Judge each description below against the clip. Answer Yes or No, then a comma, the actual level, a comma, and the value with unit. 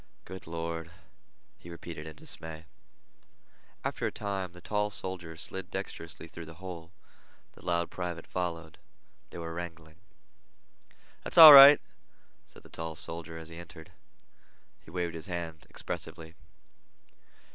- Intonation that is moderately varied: No, narrow, 1.5 semitones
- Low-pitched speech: Yes, very low, 85 Hz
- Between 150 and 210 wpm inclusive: No, slow, 135 wpm